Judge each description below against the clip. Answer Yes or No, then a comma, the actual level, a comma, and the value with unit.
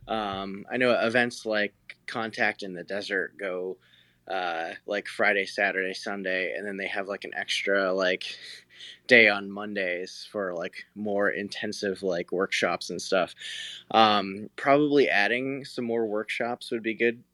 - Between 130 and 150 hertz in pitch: No, low, 105 Hz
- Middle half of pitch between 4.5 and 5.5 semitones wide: No, average, 2.9 semitones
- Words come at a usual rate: Yes, average, 150 wpm